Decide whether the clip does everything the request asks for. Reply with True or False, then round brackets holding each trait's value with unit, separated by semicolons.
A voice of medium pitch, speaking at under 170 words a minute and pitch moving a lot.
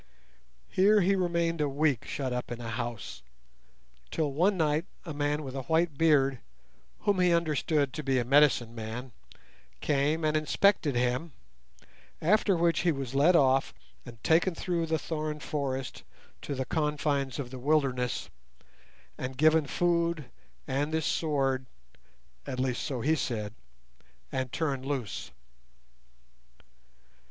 False (145 Hz; 140 wpm; 3.7 semitones)